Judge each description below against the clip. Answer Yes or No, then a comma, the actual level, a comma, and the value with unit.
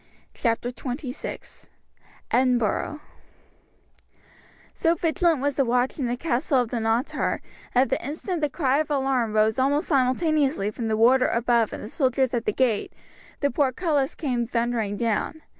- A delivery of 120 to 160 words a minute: Yes, average, 145 wpm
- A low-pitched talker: No, very high, 255 Hz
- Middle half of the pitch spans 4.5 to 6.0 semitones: No, average, 3.4 semitones